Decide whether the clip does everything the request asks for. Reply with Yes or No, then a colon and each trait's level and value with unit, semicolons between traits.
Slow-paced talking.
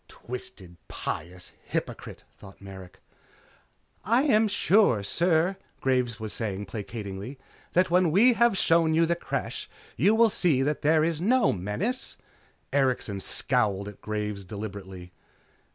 Yes: slow, 130 wpm